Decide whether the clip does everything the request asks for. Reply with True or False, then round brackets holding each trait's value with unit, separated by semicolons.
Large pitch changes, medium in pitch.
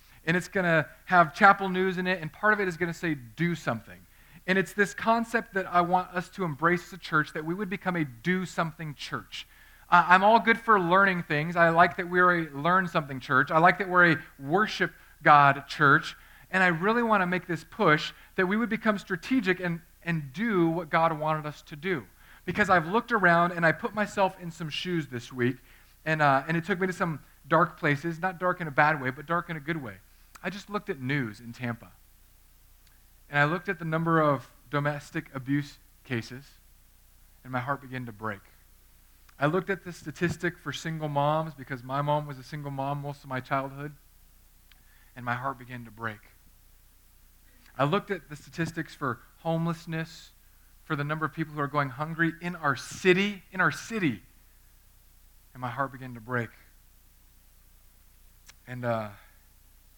True (6.0 semitones; 155 Hz)